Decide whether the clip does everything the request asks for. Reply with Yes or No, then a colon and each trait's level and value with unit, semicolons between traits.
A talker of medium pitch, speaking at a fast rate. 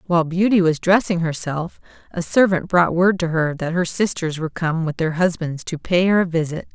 Yes: medium, 170 Hz; fast, 215 wpm